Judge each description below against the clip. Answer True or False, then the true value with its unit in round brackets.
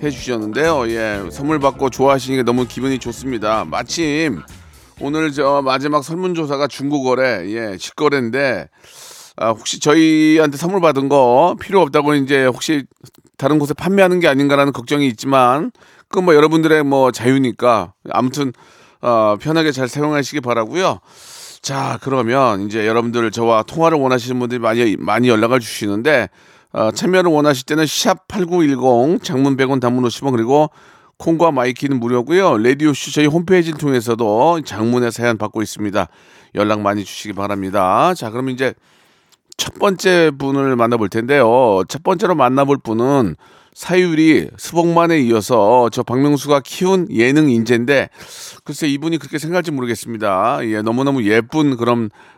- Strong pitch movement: False (4.3 semitones)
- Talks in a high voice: False (135 Hz)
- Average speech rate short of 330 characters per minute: False (335 characters per minute)